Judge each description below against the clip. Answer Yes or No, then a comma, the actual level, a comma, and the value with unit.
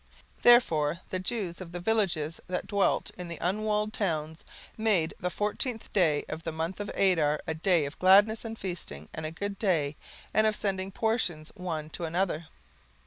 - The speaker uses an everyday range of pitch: Yes, average, 4.5 semitones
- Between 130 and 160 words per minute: No, average, 175 wpm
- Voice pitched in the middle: Yes, medium, 180 Hz